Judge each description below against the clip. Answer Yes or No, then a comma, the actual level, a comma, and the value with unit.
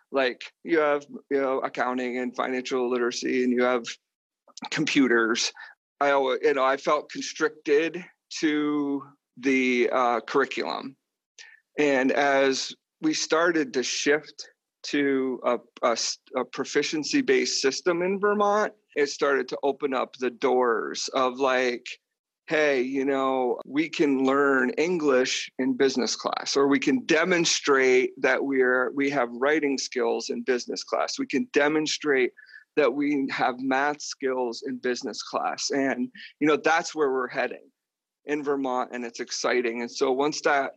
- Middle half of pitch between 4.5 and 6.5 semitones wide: No, average, 3.8 semitones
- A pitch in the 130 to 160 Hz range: Yes, medium, 140 Hz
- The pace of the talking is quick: No, average, 145 wpm